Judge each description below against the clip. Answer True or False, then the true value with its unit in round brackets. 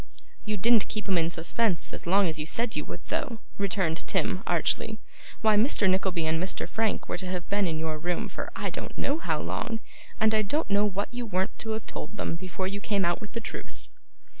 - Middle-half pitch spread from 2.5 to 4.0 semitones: True (3.7 semitones)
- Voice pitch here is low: False (200 Hz)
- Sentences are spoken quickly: True (225 wpm)